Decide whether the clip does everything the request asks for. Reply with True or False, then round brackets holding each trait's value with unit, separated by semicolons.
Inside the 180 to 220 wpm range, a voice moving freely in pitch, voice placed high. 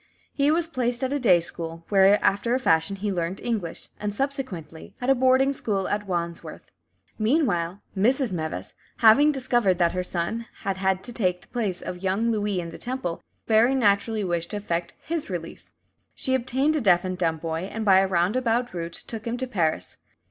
True (190 wpm; 5.7 semitones; 205 Hz)